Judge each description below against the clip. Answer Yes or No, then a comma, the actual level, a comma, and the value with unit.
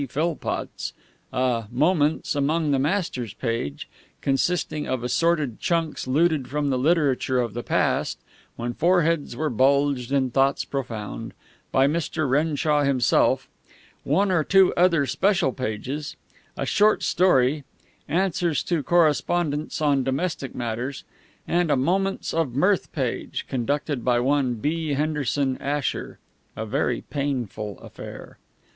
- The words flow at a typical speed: No, slow, 125 wpm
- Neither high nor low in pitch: Yes, medium, 145 Hz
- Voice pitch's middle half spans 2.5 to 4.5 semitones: Yes, average, 4.2 semitones